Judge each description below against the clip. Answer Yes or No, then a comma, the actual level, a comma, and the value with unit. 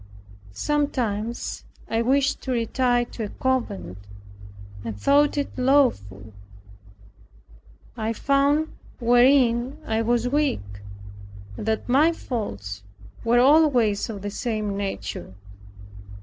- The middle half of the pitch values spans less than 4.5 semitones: No, average, 4.8 semitones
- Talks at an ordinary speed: No, slow, 105 wpm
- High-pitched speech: Yes, high, 235 Hz